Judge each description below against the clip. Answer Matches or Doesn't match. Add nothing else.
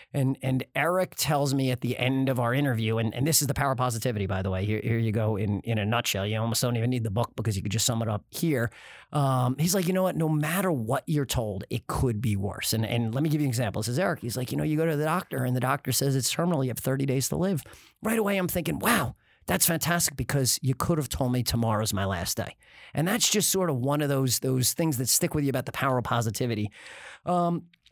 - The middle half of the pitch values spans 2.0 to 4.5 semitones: Doesn't match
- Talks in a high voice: Doesn't match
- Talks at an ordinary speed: Doesn't match